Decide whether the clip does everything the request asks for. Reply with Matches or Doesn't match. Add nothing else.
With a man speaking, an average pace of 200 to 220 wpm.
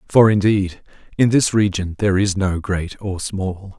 Doesn't match